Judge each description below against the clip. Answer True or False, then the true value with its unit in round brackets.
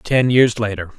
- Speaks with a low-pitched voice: True (110 Hz)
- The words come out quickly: False (185 wpm)